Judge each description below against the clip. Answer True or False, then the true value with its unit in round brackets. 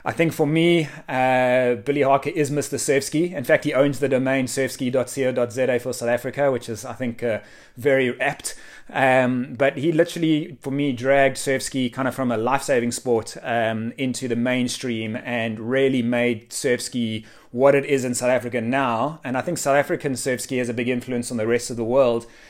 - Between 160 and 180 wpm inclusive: False (195 wpm)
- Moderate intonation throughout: False (2.3 semitones)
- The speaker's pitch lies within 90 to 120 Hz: False (130 Hz)